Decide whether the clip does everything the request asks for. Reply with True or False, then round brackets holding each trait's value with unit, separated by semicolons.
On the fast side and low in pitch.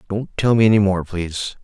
True (220 wpm; 100 Hz)